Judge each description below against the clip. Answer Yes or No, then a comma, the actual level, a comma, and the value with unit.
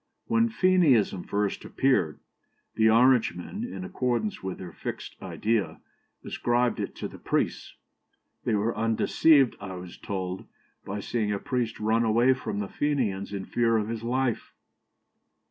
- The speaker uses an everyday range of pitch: Yes, average, 4.4 semitones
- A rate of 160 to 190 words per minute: No, average, 145 wpm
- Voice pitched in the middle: No, low, 115 Hz